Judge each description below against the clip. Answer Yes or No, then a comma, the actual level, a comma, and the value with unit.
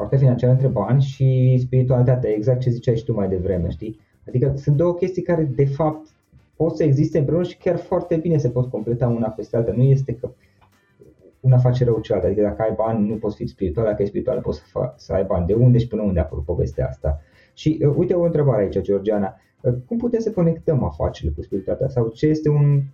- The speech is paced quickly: Yes, fast, 220 wpm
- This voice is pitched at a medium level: No, low, 125 Hz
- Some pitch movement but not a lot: No, wide, 5.7 semitones